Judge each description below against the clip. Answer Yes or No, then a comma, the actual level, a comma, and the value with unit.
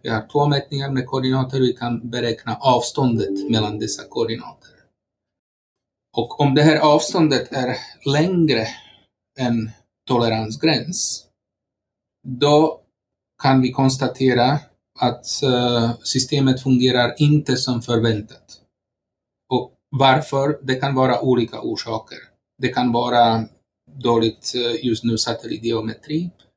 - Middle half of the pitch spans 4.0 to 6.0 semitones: No, average, 2.9 semitones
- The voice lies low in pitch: Yes, low, 125 Hz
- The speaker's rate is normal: No, slow, 110 wpm